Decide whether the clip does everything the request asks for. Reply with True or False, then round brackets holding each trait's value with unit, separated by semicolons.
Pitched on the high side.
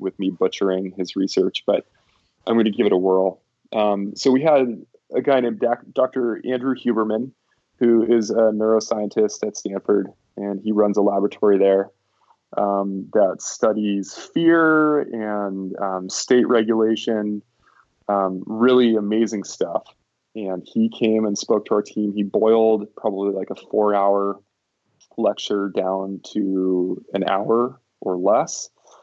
False (105 Hz)